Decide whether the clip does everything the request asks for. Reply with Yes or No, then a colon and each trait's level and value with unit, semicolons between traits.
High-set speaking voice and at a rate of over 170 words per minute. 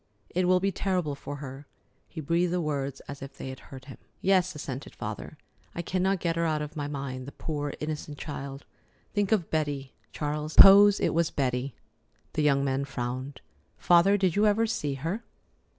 No: medium, 150 Hz; average, 185 wpm